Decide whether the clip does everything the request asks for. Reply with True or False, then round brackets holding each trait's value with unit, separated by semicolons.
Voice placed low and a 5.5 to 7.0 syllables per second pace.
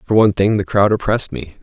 True (100 Hz; 6.7 syllables/s)